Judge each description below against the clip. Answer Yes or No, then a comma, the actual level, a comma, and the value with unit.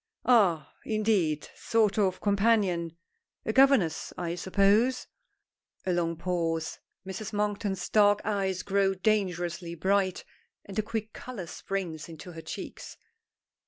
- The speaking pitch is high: Yes, high, 195 Hz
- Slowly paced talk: Yes, slow, 120 wpm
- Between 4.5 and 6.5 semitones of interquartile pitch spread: No, average, 3.5 semitones